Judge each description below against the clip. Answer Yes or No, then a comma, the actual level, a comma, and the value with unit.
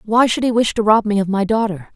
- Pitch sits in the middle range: No, high, 215 Hz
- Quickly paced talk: Yes, fast, 305 wpm